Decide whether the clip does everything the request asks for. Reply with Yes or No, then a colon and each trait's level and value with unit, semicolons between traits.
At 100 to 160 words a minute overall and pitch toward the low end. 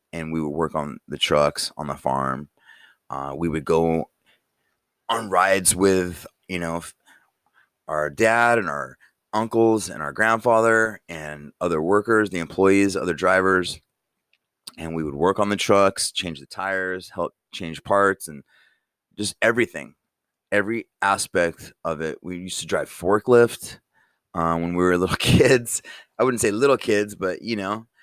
Yes: average, 155 wpm; very low, 95 Hz